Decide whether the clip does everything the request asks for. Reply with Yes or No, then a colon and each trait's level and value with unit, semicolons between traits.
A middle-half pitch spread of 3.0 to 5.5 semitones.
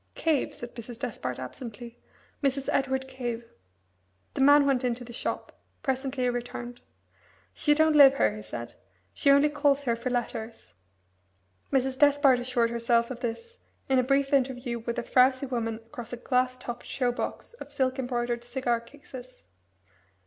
No: narrow, 2.5 semitones